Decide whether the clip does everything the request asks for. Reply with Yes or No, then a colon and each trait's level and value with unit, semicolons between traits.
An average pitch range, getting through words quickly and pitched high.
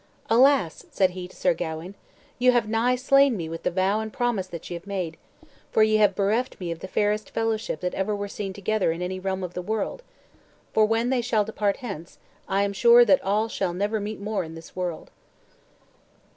Yes: average, 3.4 semitones; fast, 215 wpm; high, 200 Hz